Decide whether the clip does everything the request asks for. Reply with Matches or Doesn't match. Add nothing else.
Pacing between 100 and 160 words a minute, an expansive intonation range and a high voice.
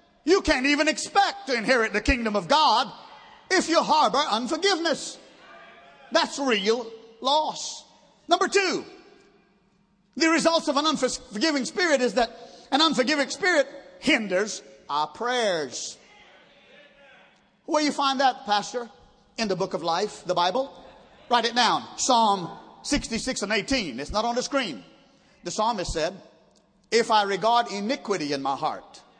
Matches